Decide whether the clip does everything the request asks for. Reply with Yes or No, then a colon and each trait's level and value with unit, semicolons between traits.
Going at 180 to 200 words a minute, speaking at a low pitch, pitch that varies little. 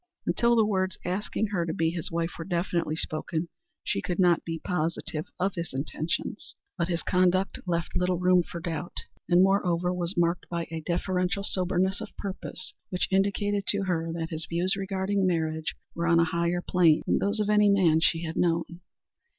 No: average, 185 wpm; medium, 175 Hz; narrow, 2.3 semitones